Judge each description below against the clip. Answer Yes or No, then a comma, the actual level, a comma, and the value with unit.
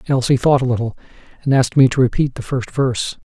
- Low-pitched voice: Yes, low, 130 Hz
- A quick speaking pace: Yes, fast, 220 wpm